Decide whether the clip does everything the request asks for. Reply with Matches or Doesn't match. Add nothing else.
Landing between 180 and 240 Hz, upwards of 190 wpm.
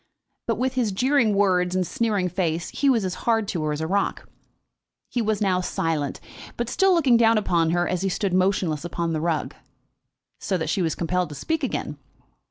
Matches